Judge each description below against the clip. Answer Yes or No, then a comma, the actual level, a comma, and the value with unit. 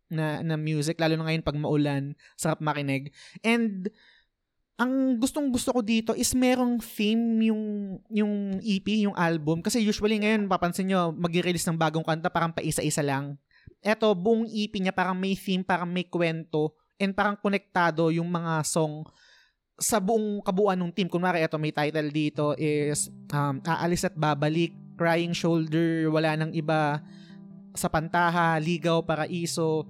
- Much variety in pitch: No, average, 4.4 semitones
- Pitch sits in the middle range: Yes, medium, 175 Hz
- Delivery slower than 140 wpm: No, fast, 155 wpm